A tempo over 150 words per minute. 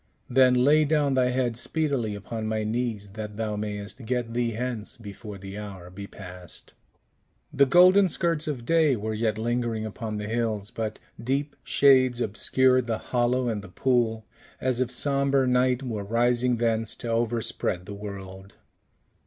Yes: average, 160 wpm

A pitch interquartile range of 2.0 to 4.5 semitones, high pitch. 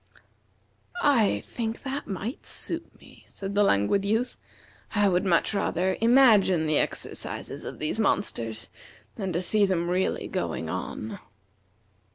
Yes: average, 4.0 semitones; high, 195 Hz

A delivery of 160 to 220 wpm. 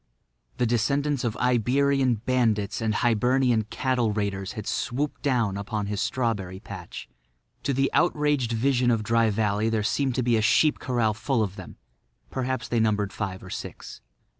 Yes: average, 165 wpm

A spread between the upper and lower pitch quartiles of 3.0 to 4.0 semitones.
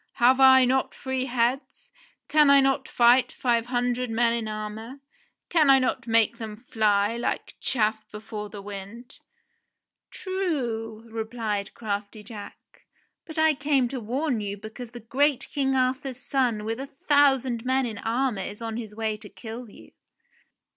Yes: average, 3.3 semitones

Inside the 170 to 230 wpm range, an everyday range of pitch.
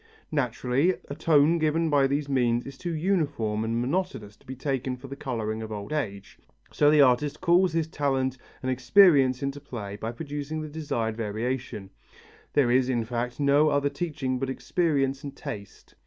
Yes: average, 175 wpm; average, 3.8 semitones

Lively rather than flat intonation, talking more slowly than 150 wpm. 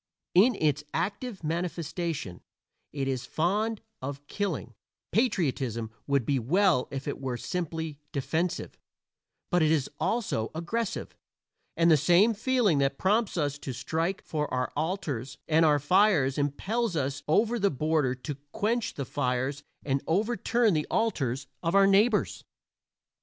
Yes: wide, 6.3 semitones; average, 140 wpm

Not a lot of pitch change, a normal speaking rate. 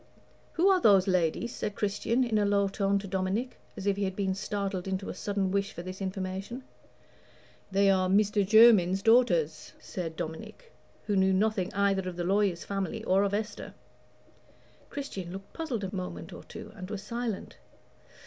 Yes: narrow, 2.1 semitones; average, 175 wpm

